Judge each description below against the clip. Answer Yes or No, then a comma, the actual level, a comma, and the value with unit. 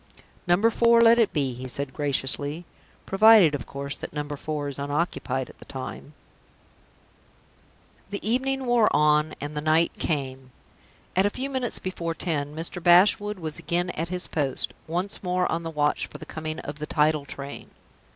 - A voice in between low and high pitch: Yes, medium, 160 Hz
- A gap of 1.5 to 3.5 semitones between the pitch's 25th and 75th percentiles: No, average, 4.5 semitones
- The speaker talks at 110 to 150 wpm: No, average, 170 wpm